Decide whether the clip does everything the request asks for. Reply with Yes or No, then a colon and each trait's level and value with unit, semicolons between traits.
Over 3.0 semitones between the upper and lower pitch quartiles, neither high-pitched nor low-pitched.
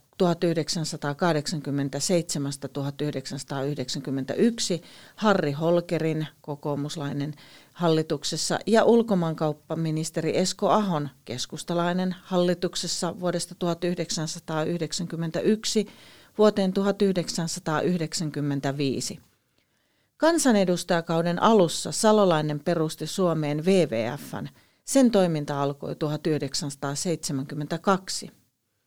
Yes: average, 3.6 semitones; medium, 165 Hz